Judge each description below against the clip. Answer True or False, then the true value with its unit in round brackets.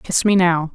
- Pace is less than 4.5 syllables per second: True (4.3 syllables/s)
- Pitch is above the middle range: False (175 Hz)